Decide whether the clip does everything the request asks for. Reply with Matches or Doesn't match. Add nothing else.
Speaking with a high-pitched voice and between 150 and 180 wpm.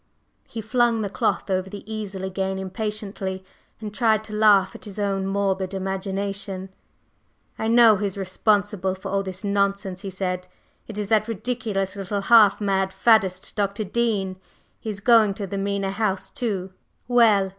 Matches